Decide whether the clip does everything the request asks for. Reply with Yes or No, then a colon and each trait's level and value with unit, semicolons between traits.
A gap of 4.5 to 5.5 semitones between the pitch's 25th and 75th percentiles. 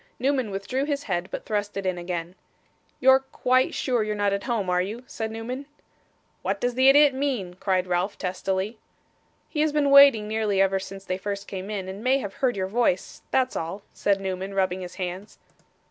Yes: average, 5.2 semitones